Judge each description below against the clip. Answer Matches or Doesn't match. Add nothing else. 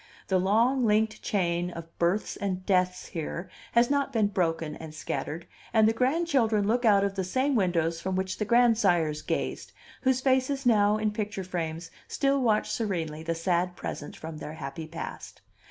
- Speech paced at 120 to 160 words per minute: Doesn't match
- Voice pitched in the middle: Doesn't match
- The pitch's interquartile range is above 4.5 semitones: Matches